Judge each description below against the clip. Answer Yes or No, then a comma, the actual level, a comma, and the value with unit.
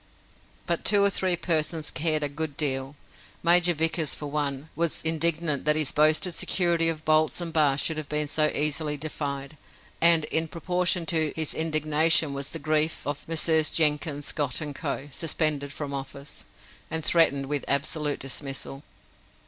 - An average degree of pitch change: No, narrow, 2.1 semitones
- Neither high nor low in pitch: Yes, medium, 155 Hz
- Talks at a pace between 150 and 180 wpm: Yes, average, 160 wpm